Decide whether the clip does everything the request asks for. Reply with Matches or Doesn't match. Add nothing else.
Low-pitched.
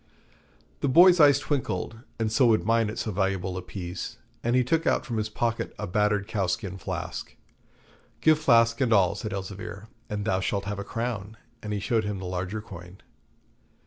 Matches